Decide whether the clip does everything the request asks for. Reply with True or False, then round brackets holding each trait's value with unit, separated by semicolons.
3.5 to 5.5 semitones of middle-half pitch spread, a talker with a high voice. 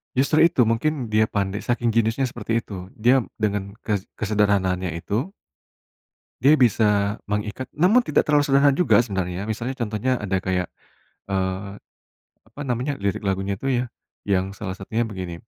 False (4.1 semitones; 105 Hz)